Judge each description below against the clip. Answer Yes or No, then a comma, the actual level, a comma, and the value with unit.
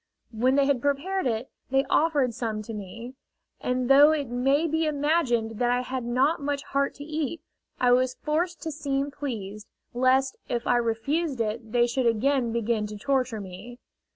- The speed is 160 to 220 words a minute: Yes, average, 180 wpm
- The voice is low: No, very high, 255 Hz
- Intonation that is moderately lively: Yes, average, 3.5 semitones